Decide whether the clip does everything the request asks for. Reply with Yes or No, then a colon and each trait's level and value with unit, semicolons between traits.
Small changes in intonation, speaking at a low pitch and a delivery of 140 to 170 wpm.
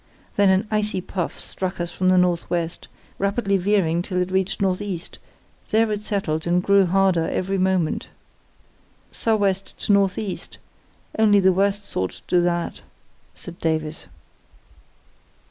No: narrow, 2.2 semitones; high, 190 Hz; average, 145 wpm